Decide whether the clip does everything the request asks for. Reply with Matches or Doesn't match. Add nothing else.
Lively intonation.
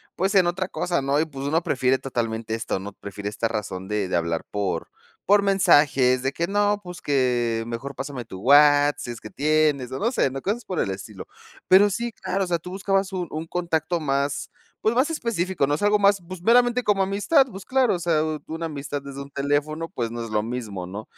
Matches